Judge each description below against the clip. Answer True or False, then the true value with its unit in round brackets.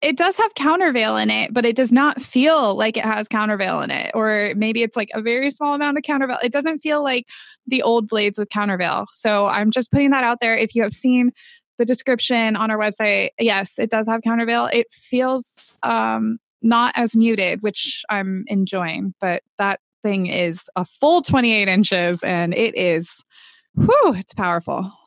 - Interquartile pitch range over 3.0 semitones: True (4.3 semitones)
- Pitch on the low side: False (225 Hz)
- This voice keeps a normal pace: True (190 wpm)